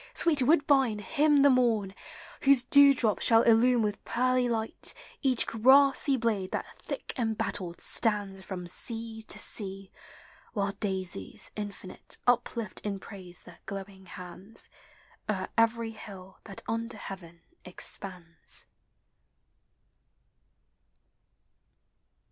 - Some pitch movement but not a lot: Yes, average, 4.2 semitones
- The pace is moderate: No, slow, 105 wpm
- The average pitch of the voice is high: Yes, high, 220 Hz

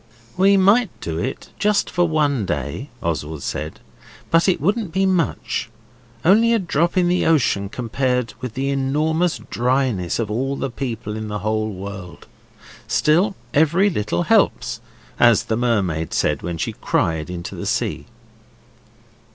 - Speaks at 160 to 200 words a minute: No, average, 150 wpm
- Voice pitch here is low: Yes, low, 130 Hz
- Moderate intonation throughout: No, wide, 8.9 semitones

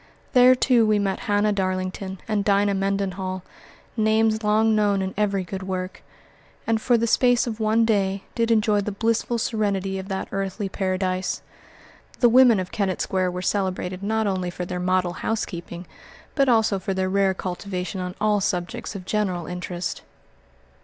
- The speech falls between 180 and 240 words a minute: No, average, 165 wpm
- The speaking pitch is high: Yes, high, 195 Hz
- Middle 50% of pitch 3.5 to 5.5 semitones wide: No, average, 2.7 semitones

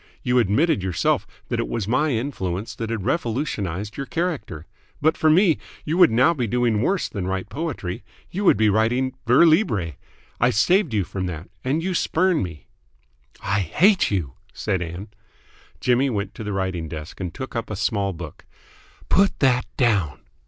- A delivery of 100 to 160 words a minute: No, average, 175 wpm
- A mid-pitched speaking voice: No, low, 110 Hz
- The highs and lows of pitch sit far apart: Yes, wide, 7.7 semitones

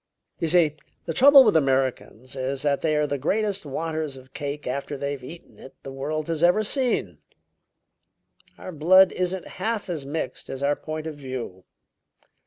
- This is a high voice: No, medium, 150 Hz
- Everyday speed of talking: Yes, average, 170 wpm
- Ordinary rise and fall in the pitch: Yes, average, 4.4 semitones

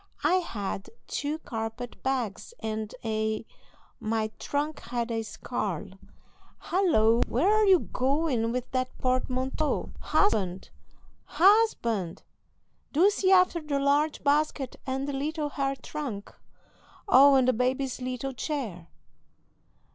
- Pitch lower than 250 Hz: No, very high, 260 Hz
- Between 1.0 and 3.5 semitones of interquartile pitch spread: No, average, 5.2 semitones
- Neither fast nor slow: No, slow, 115 wpm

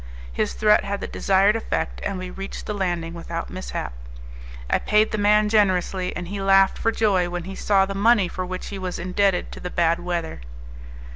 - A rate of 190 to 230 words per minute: Yes, average, 200 wpm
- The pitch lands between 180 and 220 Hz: Yes, high, 190 Hz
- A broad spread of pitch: No, narrow, 2.4 semitones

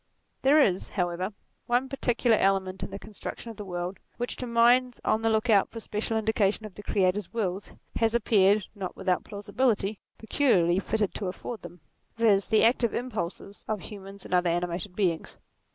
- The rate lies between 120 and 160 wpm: No, average, 175 wpm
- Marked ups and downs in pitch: No, average, 3.4 semitones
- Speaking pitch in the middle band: No, high, 210 Hz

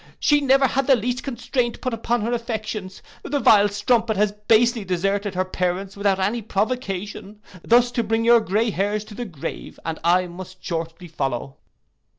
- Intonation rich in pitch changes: No, average, 4.0 semitones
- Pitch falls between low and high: No, high, 210 Hz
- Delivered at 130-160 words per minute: No, average, 170 wpm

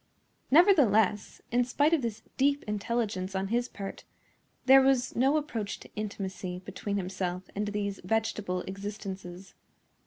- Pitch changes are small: No, average, 4.3 semitones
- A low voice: No, high, 210 Hz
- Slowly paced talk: Yes, slow, 130 wpm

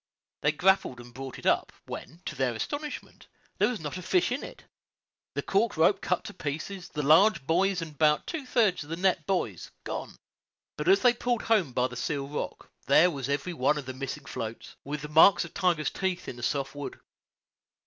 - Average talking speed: No, fast, 210 wpm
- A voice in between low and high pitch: Yes, medium, 160 Hz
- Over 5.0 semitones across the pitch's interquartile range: Yes, wide, 5.4 semitones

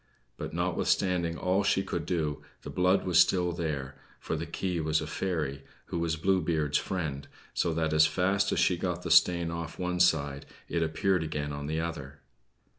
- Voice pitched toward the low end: Yes, very low, 85 Hz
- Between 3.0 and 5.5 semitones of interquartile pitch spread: No, narrow, 2.6 semitones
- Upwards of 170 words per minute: Yes, average, 190 wpm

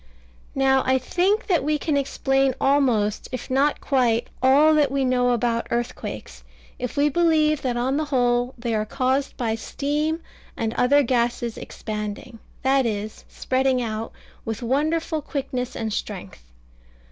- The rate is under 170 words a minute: Yes, average, 145 wpm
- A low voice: No, very high, 260 Hz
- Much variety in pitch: No, average, 3.4 semitones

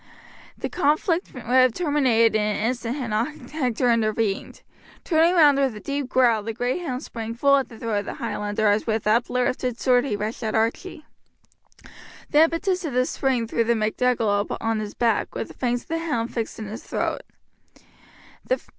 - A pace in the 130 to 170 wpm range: No, average, 185 wpm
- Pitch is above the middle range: Yes, high, 240 Hz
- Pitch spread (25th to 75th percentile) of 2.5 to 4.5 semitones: Yes, average, 4.0 semitones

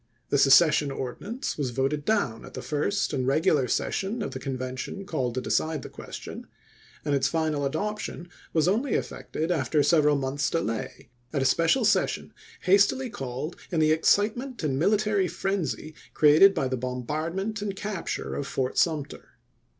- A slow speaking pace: No, average, 160 wpm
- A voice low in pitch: No, medium, 155 Hz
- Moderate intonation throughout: No, wide, 6.4 semitones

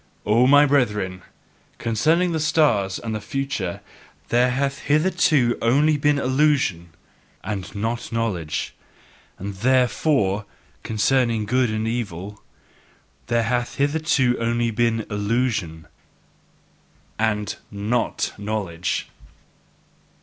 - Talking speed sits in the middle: No, slow, 100 wpm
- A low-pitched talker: Yes, low, 115 Hz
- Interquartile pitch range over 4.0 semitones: Yes, average, 4.9 semitones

